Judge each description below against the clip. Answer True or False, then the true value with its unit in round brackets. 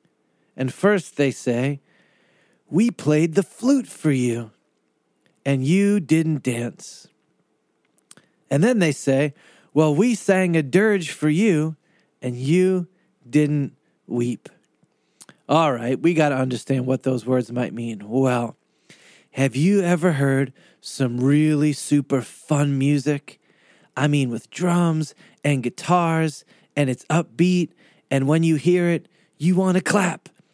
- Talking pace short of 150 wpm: True (135 wpm)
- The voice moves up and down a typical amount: True (4.9 semitones)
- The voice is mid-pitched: True (150 Hz)